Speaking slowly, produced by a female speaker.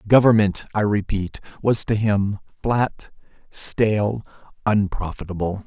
No: slow, 95 wpm; male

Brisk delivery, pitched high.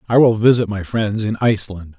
No: fast, 210 wpm; low, 105 Hz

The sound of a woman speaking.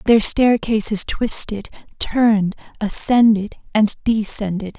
Yes: female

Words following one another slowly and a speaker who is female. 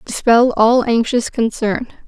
Yes: slow, 115 wpm; female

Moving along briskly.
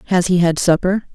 Yes: fast, 210 wpm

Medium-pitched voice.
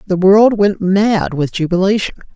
No: high, 195 Hz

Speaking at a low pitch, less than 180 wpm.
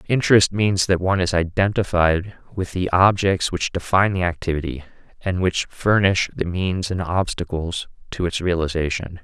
Yes: very low, 90 Hz; average, 150 wpm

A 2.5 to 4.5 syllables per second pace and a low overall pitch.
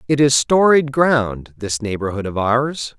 Yes: 4.0 syllables/s; low, 125 Hz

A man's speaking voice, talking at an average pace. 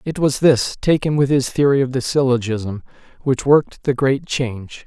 Yes: male; average, 185 wpm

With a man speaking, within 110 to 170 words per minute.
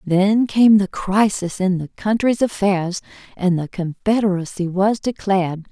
No: female; slow, 135 wpm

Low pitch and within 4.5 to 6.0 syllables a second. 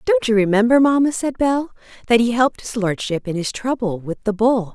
No: high, 225 Hz; 5.4 syllables/s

